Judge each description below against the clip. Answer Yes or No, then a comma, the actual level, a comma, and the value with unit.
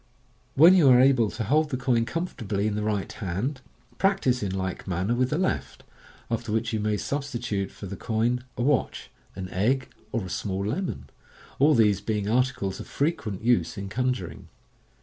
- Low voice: Yes, low, 115 Hz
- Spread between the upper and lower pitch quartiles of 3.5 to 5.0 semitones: Yes, average, 4.5 semitones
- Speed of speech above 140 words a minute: Yes, average, 190 wpm